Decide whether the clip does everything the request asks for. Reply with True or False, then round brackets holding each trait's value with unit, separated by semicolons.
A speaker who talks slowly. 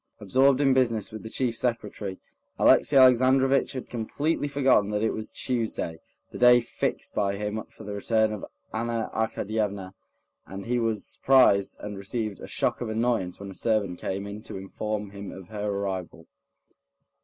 False (165 wpm)